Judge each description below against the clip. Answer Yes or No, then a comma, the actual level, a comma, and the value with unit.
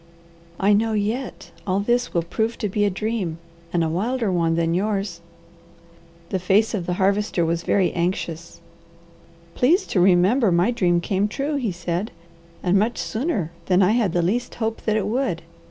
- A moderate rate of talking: Yes, average, 175 wpm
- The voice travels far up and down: No, average, 4.1 semitones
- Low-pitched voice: No, high, 195 Hz